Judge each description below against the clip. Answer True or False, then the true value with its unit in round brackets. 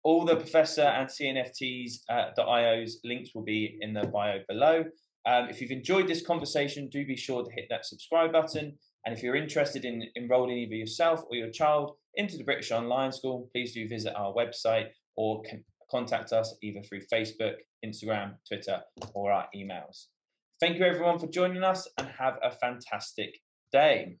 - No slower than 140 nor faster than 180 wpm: True (175 wpm)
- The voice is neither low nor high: False (125 Hz)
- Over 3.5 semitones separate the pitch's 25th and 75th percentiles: True (5.1 semitones)